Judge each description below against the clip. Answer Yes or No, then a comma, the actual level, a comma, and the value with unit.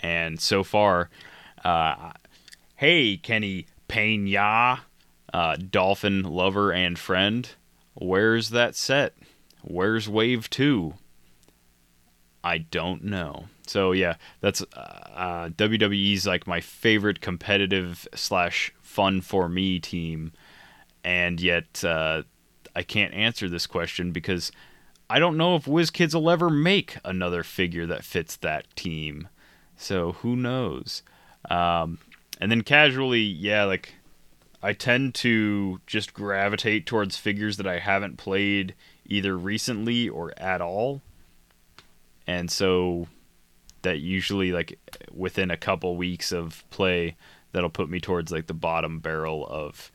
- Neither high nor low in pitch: No, very low, 95 Hz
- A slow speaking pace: Yes, slow, 125 wpm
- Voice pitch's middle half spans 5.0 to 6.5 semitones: No, average, 3.6 semitones